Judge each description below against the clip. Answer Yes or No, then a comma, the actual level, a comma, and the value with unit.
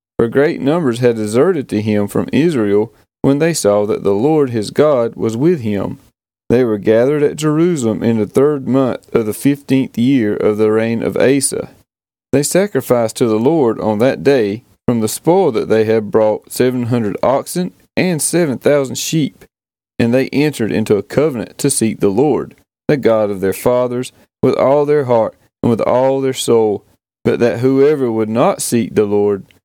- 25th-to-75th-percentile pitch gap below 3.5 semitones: No, average, 4.3 semitones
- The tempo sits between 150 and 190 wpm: Yes, average, 185 wpm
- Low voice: Yes, low, 120 Hz